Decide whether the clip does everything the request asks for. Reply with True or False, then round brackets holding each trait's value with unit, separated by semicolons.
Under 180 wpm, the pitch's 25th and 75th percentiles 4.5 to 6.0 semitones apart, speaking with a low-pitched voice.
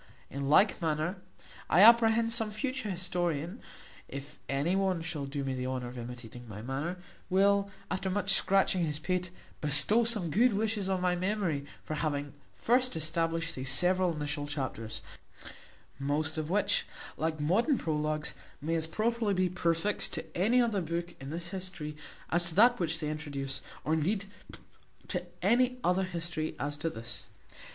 False (160 wpm; 4.8 semitones; 170 Hz)